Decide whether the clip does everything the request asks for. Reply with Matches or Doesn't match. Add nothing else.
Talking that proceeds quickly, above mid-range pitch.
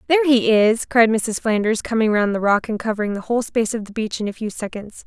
Matches